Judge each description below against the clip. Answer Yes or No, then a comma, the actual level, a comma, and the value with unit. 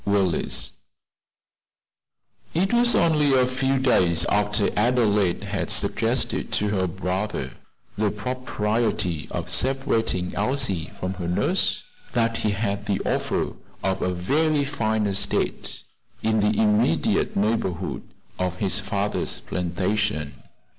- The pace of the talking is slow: Yes, slow, 115 wpm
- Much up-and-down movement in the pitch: No, average, 4.6 semitones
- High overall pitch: No, low, 105 Hz